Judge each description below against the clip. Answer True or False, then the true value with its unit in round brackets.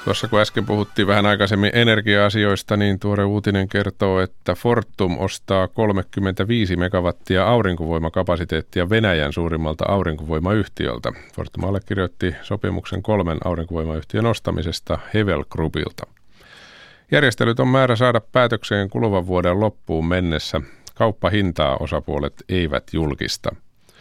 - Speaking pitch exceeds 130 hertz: False (95 Hz)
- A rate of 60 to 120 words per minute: True (100 wpm)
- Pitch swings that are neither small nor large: True (3.5 semitones)